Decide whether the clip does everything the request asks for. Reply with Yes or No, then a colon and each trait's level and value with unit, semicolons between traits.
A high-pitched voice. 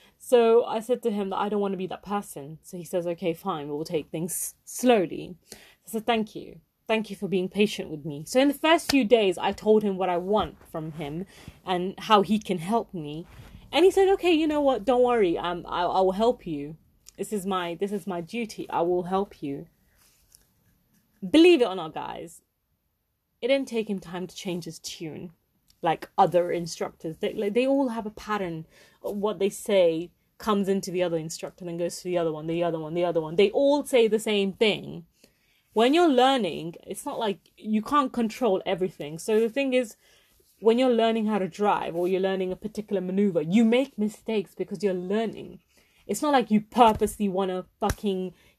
Yes: high, 195 Hz